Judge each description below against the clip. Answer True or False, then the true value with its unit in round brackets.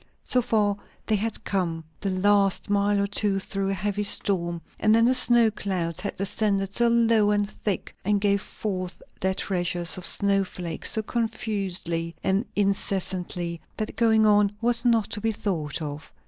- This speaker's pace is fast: False (175 wpm)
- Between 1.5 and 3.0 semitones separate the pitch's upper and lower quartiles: True (2.6 semitones)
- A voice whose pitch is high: True (200 Hz)